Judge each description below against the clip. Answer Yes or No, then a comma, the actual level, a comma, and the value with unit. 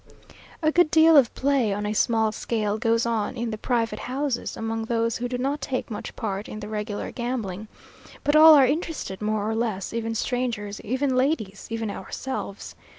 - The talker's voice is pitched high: Yes, high, 230 Hz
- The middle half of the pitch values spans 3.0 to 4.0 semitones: Yes, average, 3.5 semitones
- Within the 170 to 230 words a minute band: Yes, average, 185 wpm